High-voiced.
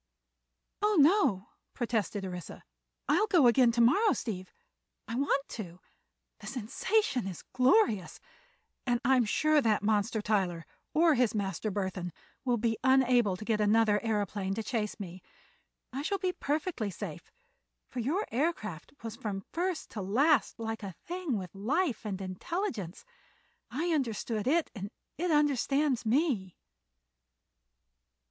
Yes: high, 230 Hz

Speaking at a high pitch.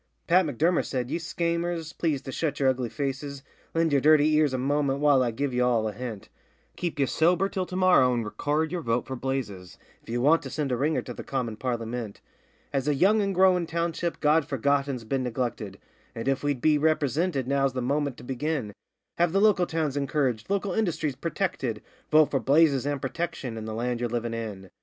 No: medium, 140 Hz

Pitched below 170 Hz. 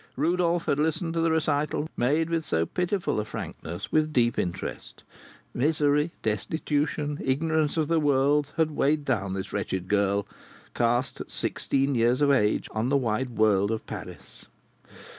Yes: medium, 140 Hz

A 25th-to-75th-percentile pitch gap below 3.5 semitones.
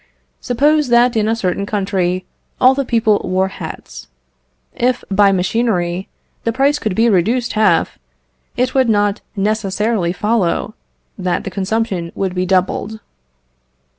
No: average, 3.9 semitones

